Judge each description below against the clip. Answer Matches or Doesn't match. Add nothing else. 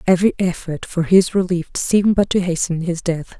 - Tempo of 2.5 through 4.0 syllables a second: Doesn't match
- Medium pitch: Matches